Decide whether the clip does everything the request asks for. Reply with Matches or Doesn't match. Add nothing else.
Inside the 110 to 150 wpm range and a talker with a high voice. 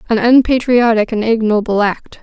Matches